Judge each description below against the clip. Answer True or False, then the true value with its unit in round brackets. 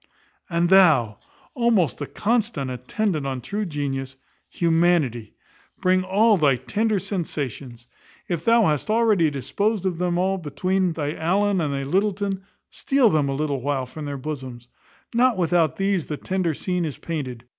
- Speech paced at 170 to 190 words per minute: False (155 wpm)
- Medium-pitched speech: True (170 Hz)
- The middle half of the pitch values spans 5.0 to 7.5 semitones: True (5.6 semitones)